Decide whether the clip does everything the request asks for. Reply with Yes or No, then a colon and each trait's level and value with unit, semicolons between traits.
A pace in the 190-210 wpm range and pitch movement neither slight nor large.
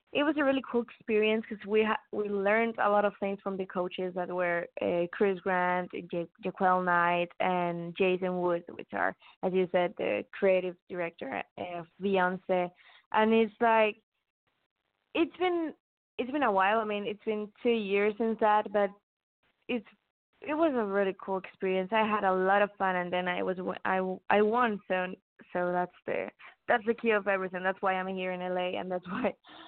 Yes: average, 195 wpm; average, 3.1 semitones